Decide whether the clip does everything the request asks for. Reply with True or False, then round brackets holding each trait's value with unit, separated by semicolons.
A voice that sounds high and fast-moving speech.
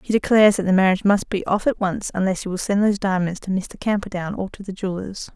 True (195 Hz; 260 wpm)